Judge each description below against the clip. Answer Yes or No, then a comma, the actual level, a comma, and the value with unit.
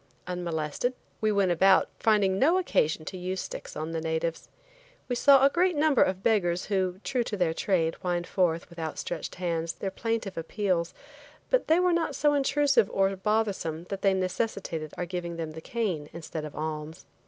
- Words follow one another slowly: No, average, 180 wpm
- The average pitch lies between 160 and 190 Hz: Yes, medium, 185 Hz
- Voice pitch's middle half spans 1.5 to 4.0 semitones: No, average, 5.1 semitones